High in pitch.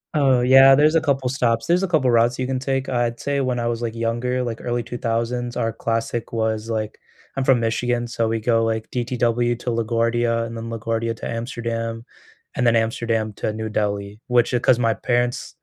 No: low, 120 Hz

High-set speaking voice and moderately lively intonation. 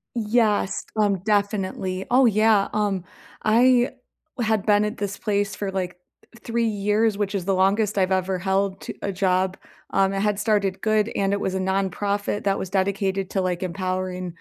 No: high, 200 Hz; narrow, 1.8 semitones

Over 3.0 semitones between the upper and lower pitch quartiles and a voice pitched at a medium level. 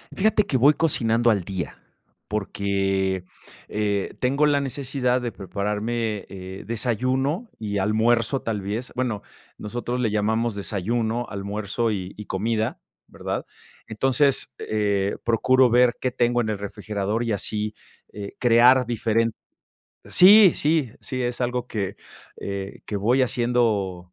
No: average, 3.5 semitones; low, 115 Hz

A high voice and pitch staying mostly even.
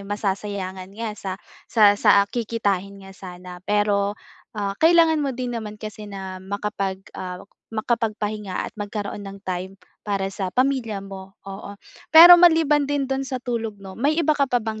No: high, 210 Hz; average, 4.0 semitones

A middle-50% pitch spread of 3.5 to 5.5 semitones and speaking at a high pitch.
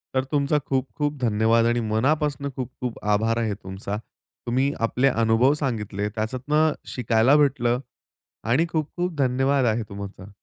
No: average, 4.1 semitones; low, 125 Hz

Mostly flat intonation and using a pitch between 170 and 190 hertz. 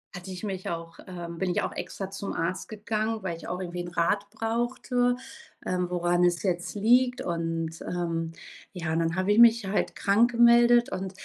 No: average, 4.4 semitones; medium, 185 Hz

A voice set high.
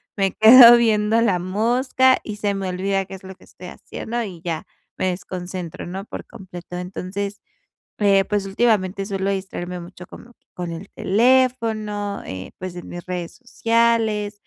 Yes: high, 195 Hz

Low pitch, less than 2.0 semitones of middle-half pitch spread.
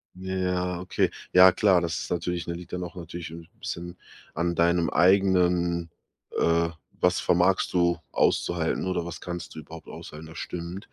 Yes: very low, 85 Hz; narrow, 1.3 semitones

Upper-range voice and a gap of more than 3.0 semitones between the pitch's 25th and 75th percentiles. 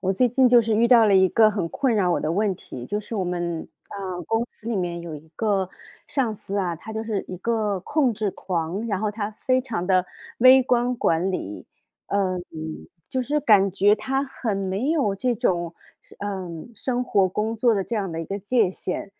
Yes: high, 205 Hz; average, 4.0 semitones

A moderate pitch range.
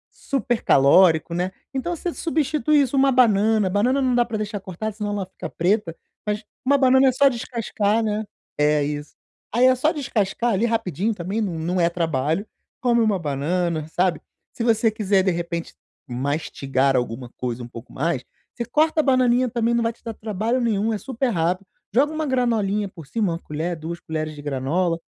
No: wide, 6.3 semitones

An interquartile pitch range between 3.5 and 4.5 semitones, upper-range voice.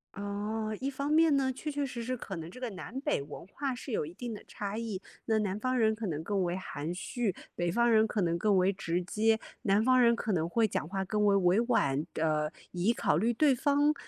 No: average, 5.1 semitones; high, 215 Hz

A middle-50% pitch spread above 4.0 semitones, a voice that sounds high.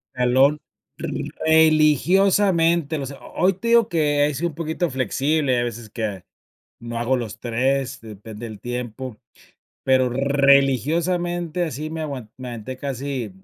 No: average, 4.5 semitones; medium, 140 Hz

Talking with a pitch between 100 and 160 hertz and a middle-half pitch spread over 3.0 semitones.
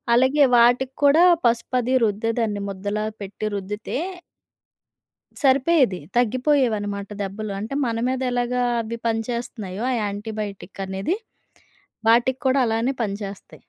No: high, 230 Hz; average, 3.7 semitones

